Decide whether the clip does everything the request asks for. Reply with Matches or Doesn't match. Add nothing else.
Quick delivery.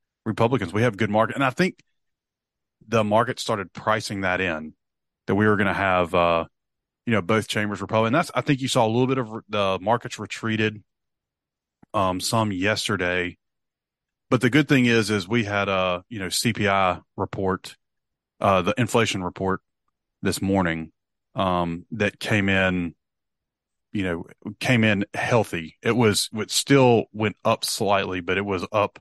Doesn't match